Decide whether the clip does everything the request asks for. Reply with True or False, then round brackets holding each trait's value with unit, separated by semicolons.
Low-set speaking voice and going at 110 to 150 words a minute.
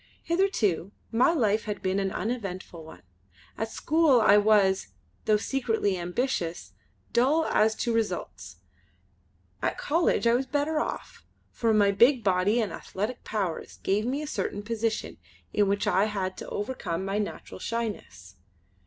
False (215 Hz; 145 wpm)